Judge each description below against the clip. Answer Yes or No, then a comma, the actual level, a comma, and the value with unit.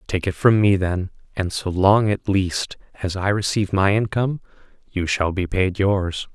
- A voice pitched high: No, very low, 95 Hz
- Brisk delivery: No, average, 190 wpm